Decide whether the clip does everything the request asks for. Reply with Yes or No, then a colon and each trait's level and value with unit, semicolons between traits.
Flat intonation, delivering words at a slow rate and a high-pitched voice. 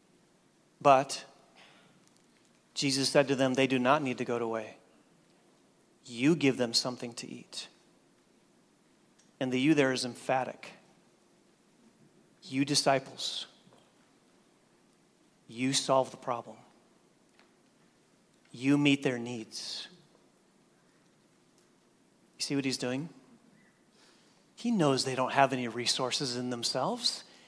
No: narrow, 2.1 semitones; slow, 105 wpm; low, 130 Hz